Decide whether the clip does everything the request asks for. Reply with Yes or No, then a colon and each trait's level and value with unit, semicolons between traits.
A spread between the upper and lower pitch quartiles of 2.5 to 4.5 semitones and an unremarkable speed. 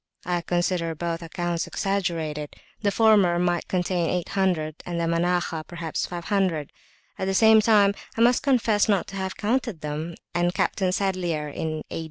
Yes: average, 2.9 semitones; average, 160 wpm